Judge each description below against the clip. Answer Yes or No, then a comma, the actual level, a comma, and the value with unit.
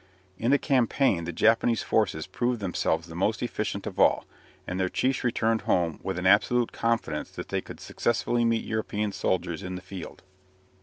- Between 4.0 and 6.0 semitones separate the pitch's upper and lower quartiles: Yes, average, 4.3 semitones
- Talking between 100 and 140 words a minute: No, average, 175 wpm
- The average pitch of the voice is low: Yes, low, 105 Hz